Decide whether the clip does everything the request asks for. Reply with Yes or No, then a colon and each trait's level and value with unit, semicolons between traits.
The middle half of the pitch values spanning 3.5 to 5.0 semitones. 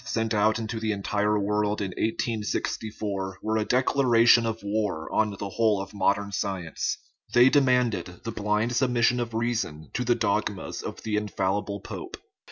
No: narrow, 2.4 semitones